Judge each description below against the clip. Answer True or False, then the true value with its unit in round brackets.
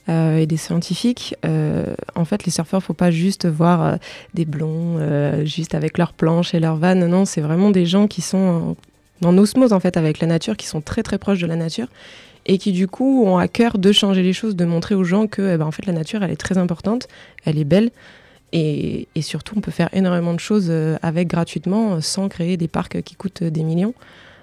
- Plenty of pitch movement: False (3.1 semitones)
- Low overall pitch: False (175 Hz)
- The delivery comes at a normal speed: False (235 wpm)